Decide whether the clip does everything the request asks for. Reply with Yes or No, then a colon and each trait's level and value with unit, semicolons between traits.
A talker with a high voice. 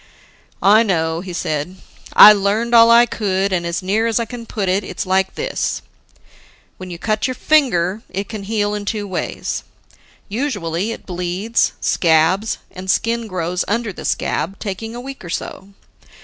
Yes: high, 200 Hz